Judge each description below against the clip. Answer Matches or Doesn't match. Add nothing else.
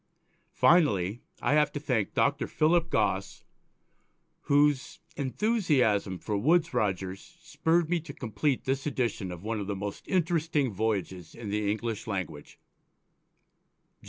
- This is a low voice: Matches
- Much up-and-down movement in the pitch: Matches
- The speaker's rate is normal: Doesn't match